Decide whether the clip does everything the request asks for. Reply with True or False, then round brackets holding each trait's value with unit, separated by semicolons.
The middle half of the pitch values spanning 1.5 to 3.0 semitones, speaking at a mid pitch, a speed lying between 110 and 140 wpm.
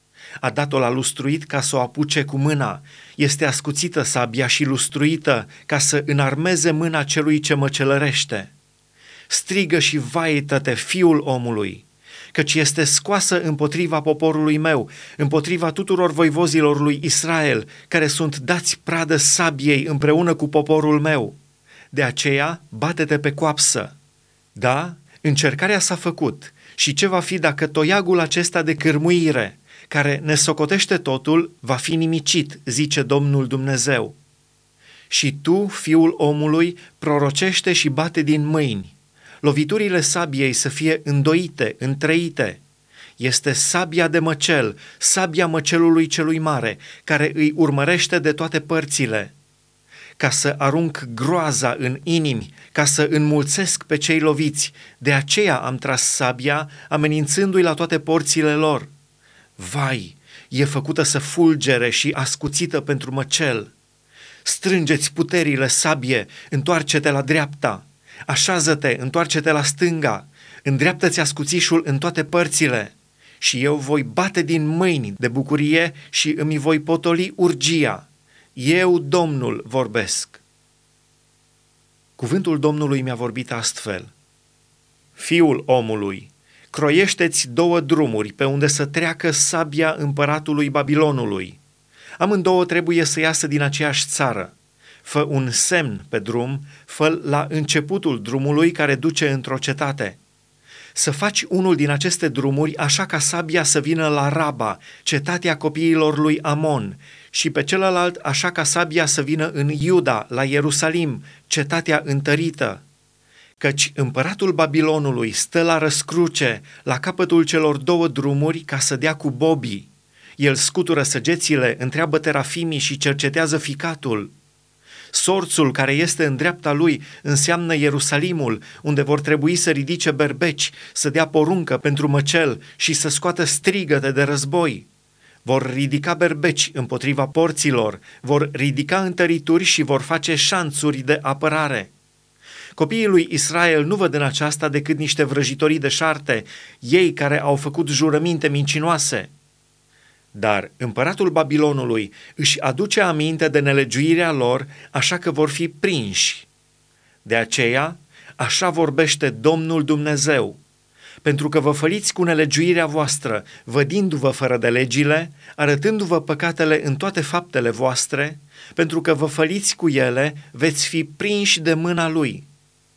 True (2.7 semitones; 150 Hz; 125 wpm)